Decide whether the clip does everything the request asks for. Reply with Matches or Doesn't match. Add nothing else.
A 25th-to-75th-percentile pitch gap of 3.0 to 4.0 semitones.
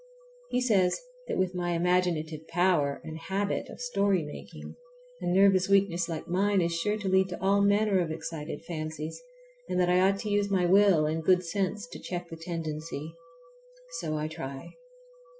Matches